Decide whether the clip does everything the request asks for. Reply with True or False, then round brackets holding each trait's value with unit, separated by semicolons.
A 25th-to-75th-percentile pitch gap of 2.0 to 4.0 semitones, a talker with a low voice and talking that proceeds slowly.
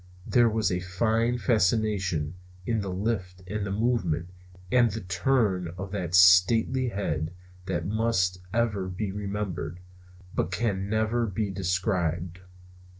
True (3.6 semitones; 95 Hz; 130 wpm)